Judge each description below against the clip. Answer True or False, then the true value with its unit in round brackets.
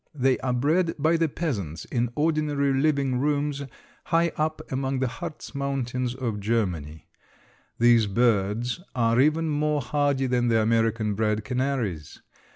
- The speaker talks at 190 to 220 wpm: False (140 wpm)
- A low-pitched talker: True (130 Hz)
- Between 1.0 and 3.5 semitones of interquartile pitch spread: False (4.4 semitones)